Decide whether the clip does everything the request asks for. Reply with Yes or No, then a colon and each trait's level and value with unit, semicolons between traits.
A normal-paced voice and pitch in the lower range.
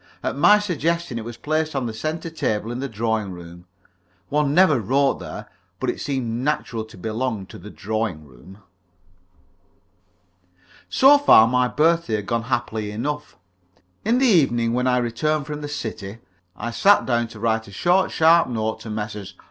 Yes: average, 170 wpm; low, 120 Hz